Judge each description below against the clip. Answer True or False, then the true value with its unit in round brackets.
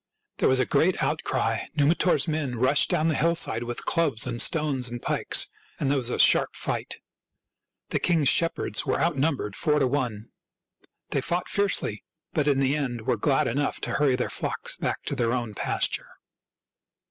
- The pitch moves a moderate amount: True (3.9 semitones)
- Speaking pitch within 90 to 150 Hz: True (140 Hz)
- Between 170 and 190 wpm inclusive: True (180 wpm)